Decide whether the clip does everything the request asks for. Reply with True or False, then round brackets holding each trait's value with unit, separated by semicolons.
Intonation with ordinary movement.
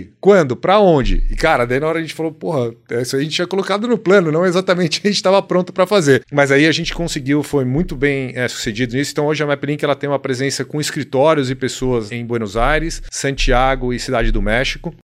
True (4.5 semitones)